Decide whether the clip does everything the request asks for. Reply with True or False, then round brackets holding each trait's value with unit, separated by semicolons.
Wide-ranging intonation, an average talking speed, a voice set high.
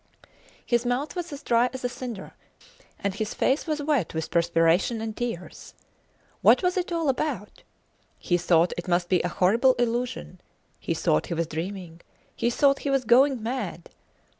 True (7.0 semitones; 170 wpm; 235 Hz)